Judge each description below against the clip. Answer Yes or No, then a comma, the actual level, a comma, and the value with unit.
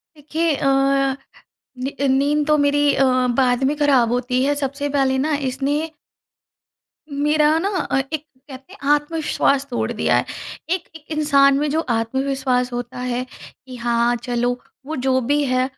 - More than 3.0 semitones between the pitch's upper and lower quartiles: No, average, 2.7 semitones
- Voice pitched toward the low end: No, very high, 275 Hz